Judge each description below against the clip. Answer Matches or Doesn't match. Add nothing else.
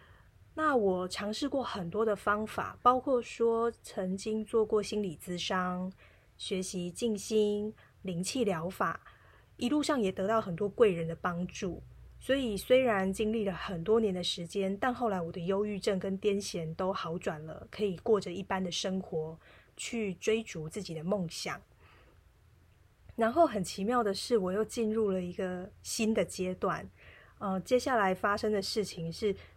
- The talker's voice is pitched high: Matches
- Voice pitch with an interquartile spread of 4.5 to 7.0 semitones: Doesn't match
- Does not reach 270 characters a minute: Matches